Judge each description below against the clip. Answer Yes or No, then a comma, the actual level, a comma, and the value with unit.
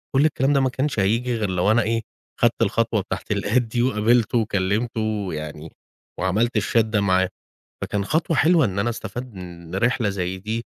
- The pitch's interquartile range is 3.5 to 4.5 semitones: Yes, average, 3.9 semitones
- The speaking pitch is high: No, low, 110 Hz